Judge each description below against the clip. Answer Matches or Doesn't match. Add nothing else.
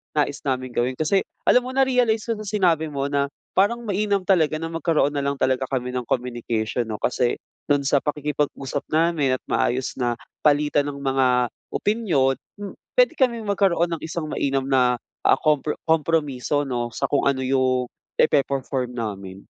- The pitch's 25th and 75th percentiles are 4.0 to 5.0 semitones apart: Matches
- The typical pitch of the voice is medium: Matches